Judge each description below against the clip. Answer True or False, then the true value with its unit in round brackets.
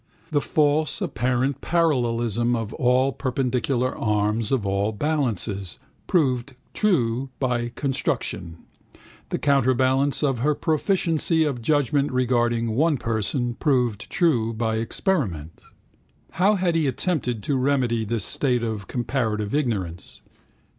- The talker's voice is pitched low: True (125 Hz)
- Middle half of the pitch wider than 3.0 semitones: True (4.1 semitones)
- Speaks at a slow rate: True (115 wpm)